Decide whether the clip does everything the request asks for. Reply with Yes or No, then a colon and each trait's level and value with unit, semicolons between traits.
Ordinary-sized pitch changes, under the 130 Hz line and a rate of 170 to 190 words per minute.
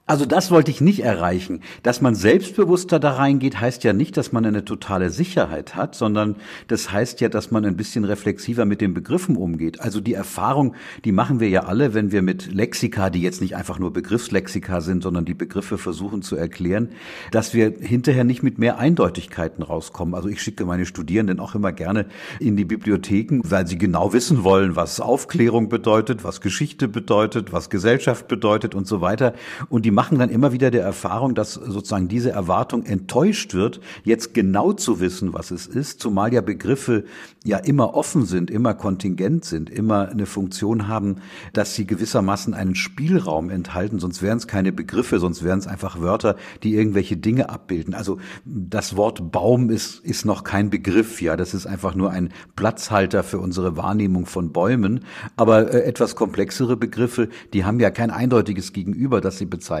Yes: average, 3.7 semitones; low, 105 Hz; average, 185 wpm